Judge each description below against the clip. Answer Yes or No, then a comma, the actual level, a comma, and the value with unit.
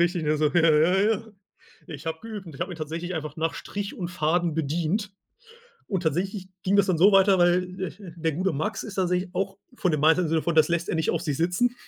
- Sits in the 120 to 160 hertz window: No, medium, 175 Hz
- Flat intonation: No, average, 3.0 semitones